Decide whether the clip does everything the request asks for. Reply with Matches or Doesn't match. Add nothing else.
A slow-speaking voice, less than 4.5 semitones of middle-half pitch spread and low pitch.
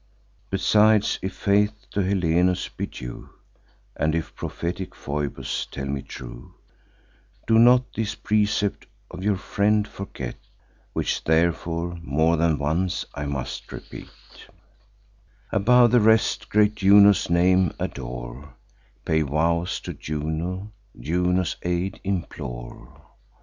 Doesn't match